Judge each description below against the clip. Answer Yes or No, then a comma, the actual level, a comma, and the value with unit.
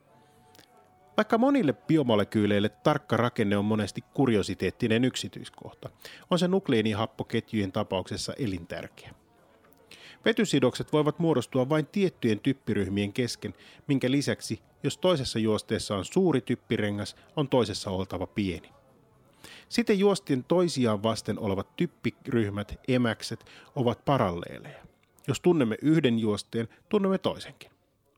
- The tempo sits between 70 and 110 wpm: Yes, average, 100 wpm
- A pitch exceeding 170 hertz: No, low, 120 Hz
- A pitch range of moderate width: No, wide, 6.3 semitones